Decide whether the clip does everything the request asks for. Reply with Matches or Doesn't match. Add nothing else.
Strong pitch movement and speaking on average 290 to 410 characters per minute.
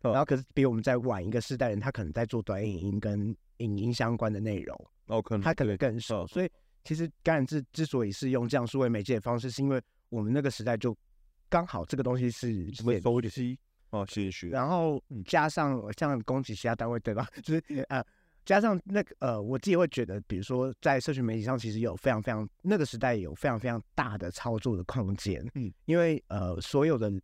Doesn't match